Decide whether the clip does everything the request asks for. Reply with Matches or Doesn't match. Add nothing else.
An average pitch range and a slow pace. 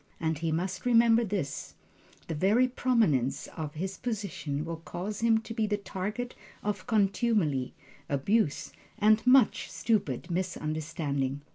Doesn't match